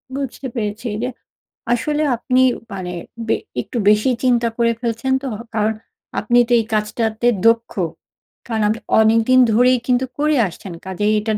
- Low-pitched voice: No, high, 230 Hz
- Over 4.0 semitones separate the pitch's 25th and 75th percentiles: No, average, 2.8 semitones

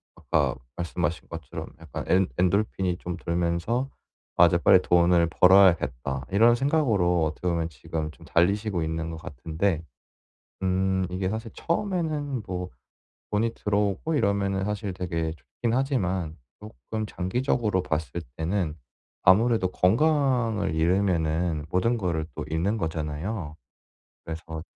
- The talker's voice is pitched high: No, very low, 90 Hz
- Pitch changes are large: No, average, 4.4 semitones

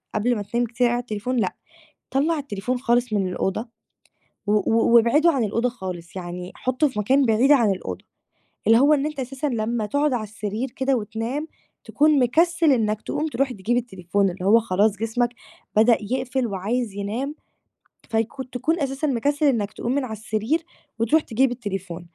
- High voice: Yes, high, 235 Hz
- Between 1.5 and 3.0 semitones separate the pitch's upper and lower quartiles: No, average, 4.3 semitones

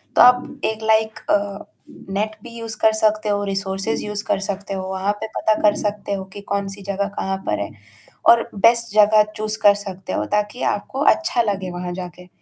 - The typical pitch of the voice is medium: No, high, 205 Hz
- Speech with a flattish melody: Yes, narrow, 2.0 semitones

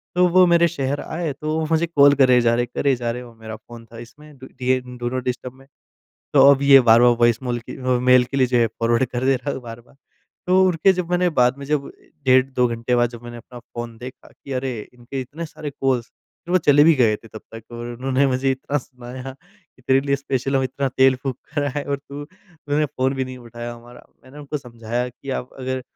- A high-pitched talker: No, low, 130 Hz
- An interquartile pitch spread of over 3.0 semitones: No, average, 2.7 semitones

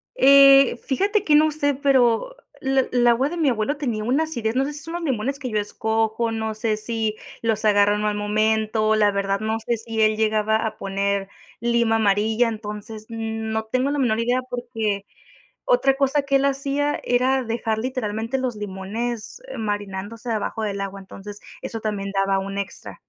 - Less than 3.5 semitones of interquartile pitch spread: No, average, 3.8 semitones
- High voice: Yes, high, 225 Hz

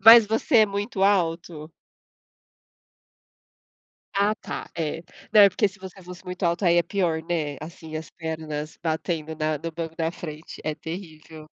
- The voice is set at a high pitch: No, medium, 165 Hz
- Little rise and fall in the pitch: No, average, 3.3 semitones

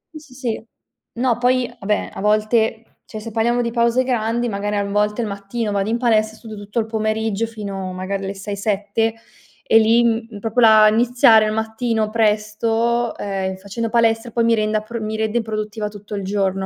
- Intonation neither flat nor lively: No, narrow, 1.9 semitones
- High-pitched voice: Yes, high, 220 Hz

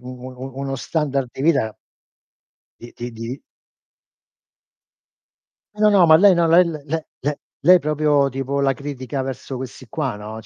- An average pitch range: Yes, average, 3.6 semitones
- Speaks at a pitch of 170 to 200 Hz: No, medium, 140 Hz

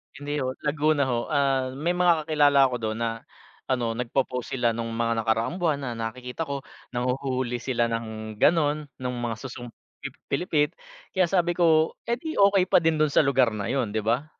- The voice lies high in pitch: No, low, 130 Hz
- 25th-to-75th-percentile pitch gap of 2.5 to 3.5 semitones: No, average, 4.6 semitones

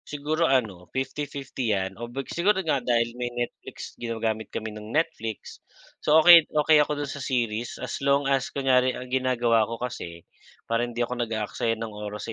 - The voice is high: No, low, 120 Hz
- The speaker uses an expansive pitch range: No, average, 3.7 semitones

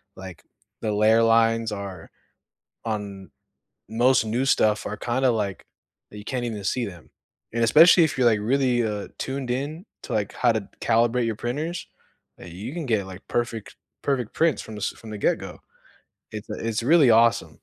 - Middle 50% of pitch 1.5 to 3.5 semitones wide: Yes, average, 3.2 semitones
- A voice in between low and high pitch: No, low, 115 Hz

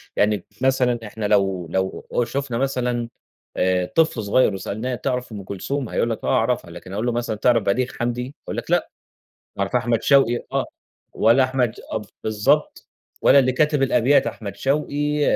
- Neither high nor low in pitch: No, low, 120 Hz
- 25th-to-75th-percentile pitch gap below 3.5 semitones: No, average, 3.8 semitones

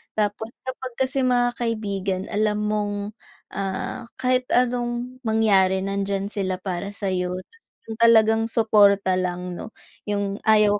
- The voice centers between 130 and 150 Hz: No, high, 210 Hz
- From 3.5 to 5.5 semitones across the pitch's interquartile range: No, average, 3.0 semitones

